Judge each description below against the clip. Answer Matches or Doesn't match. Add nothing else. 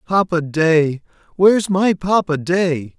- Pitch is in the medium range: Matches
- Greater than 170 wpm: Doesn't match